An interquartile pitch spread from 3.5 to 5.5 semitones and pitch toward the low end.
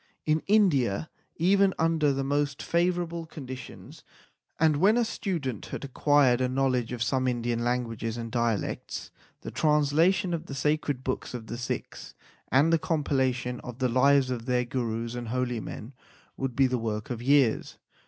Yes: average, 4.0 semitones; low, 130 Hz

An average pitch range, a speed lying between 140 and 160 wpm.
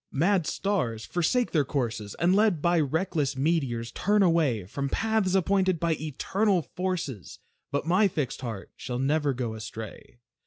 No: wide, 6.3 semitones; average, 150 wpm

